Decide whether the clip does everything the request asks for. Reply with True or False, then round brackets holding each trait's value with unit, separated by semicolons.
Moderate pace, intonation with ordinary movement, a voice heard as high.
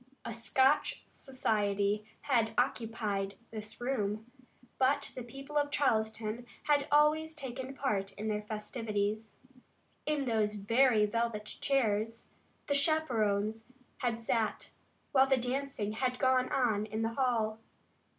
False (120 wpm; 3.9 semitones; 230 Hz)